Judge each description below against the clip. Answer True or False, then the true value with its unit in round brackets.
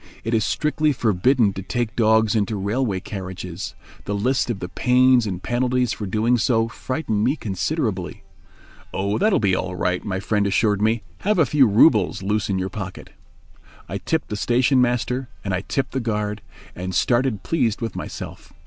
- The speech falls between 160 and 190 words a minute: True (180 wpm)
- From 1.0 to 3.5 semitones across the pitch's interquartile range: False (4.1 semitones)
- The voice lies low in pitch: True (110 Hz)